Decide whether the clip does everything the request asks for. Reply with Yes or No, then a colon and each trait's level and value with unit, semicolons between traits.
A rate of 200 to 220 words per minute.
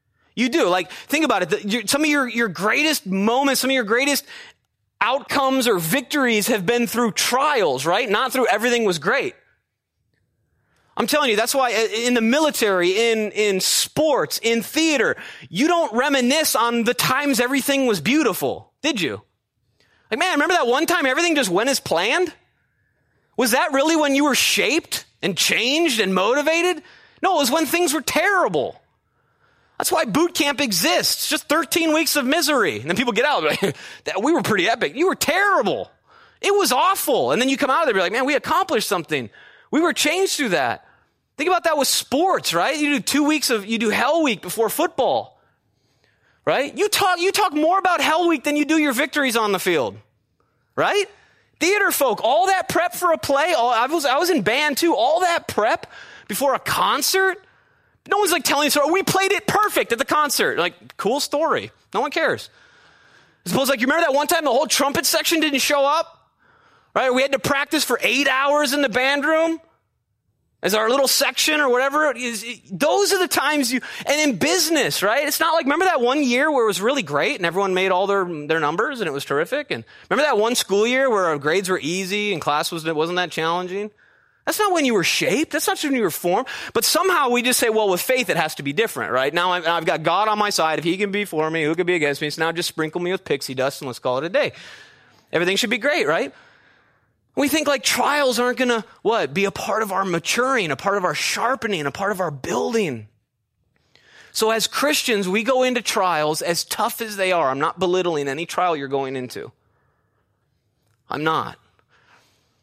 Yes: fast, 205 wpm